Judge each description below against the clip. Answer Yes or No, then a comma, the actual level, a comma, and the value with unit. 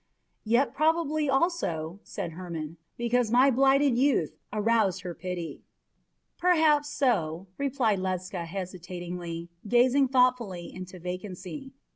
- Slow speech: Yes, slow, 105 wpm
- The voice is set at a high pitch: Yes, high, 215 Hz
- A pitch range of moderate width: No, wide, 7.2 semitones